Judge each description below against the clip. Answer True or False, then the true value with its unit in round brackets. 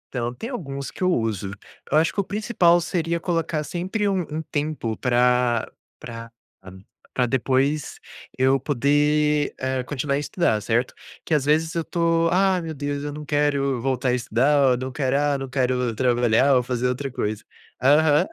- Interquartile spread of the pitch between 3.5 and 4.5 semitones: True (4.0 semitones)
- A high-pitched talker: False (140 Hz)